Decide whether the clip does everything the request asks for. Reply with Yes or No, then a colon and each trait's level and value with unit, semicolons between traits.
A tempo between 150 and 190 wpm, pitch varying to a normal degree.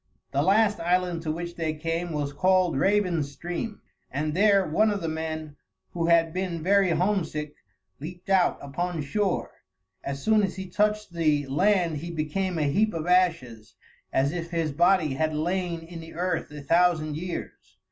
Yes: average, 170 wpm; average, 3.1 semitones